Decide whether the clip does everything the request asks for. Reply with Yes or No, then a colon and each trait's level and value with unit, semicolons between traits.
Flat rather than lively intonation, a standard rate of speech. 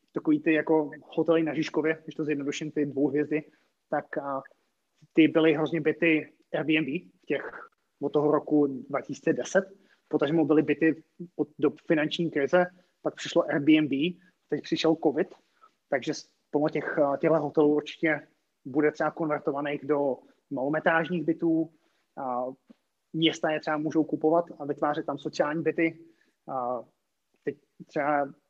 Yes: narrow, 1.7 semitones; average, 135 wpm